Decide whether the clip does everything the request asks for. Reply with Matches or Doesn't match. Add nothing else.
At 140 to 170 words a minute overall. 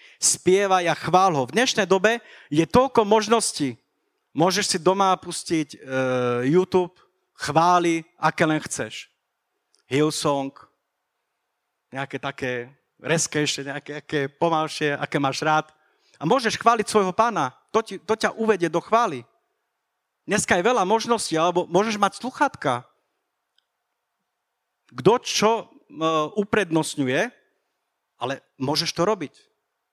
Doesn't match